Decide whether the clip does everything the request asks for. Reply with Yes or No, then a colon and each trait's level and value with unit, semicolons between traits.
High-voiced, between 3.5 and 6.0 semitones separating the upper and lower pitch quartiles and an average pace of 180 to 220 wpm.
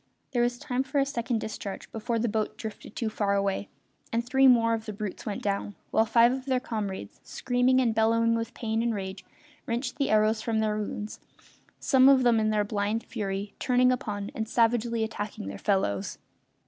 No: high, 225 Hz; average, 2.7 semitones; average, 195 wpm